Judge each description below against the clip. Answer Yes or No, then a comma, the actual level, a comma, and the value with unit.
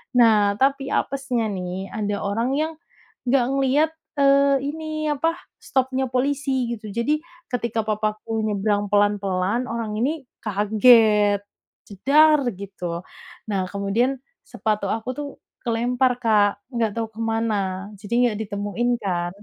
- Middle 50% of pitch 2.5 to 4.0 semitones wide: No, average, 4.4 semitones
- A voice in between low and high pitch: No, high, 225 Hz